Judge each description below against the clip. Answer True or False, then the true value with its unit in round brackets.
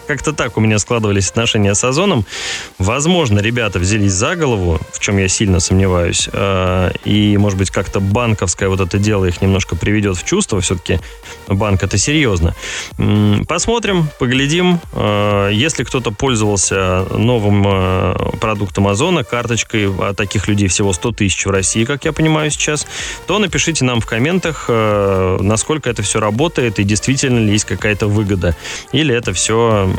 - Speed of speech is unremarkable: True (150 wpm)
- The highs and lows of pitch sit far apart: False (3.9 semitones)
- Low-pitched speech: True (105 Hz)